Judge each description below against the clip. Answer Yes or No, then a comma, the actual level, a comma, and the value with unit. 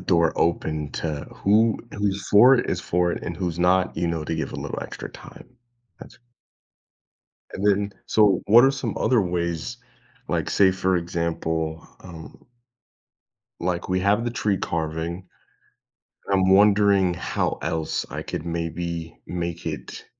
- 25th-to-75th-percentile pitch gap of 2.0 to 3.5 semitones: Yes, average, 3.2 semitones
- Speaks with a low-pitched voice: Yes, very low, 90 Hz